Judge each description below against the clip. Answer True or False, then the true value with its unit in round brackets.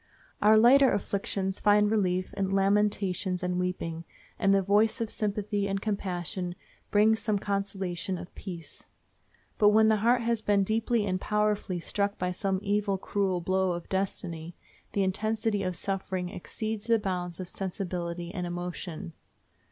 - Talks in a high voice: True (195 Hz)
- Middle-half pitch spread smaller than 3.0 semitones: True (2.5 semitones)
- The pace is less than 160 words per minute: True (145 wpm)